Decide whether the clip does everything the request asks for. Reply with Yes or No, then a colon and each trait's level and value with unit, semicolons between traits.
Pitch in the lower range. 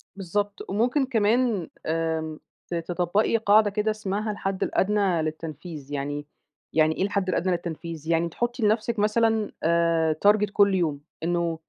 No: high, 190 Hz